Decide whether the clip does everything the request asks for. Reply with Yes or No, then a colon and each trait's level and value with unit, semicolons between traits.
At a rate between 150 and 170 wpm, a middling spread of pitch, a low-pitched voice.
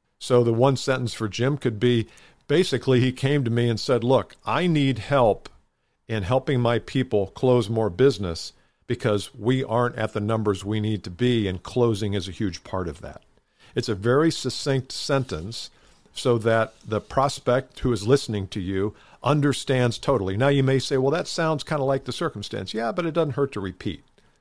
No: average, 195 wpm; average, 4.1 semitones; low, 120 Hz